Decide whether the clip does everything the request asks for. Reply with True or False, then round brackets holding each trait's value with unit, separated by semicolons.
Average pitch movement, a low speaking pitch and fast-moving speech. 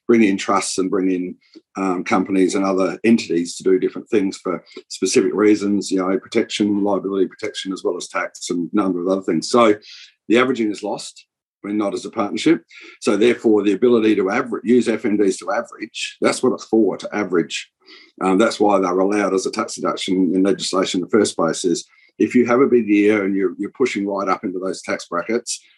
True (3.3 semitones; 100 Hz; 215 wpm)